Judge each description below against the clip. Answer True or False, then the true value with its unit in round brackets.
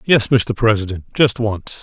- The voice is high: False (110 Hz)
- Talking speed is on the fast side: False (165 wpm)